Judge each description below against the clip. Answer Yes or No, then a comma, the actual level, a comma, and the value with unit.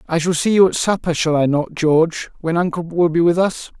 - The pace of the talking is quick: Yes, fast, 255 wpm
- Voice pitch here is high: No, medium, 165 Hz